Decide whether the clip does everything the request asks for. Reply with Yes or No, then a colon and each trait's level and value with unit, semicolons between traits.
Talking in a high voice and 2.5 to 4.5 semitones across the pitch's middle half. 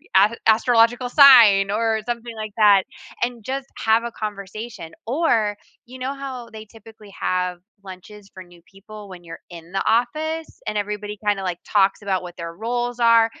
Yes: high, 215 Hz; average, 3.4 semitones